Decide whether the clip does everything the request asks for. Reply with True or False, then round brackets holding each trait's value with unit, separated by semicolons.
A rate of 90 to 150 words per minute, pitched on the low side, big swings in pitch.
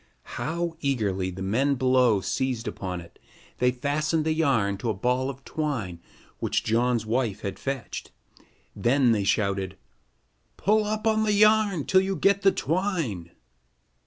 True (145 wpm; 130 Hz; 7.4 semitones)